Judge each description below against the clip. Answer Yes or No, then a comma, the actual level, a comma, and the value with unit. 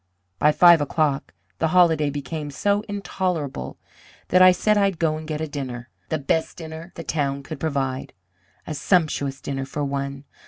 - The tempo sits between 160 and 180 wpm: Yes, average, 165 wpm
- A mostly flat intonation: No, average, 3.4 semitones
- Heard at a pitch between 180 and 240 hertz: No, medium, 155 Hz